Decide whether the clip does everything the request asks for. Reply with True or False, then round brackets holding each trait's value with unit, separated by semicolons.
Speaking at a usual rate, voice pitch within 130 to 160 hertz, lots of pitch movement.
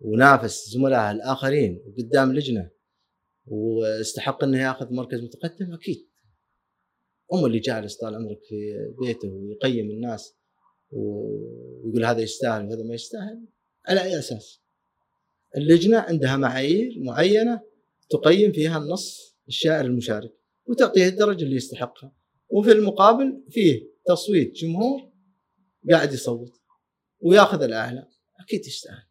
True (110 wpm; 135 Hz; 8.9 semitones)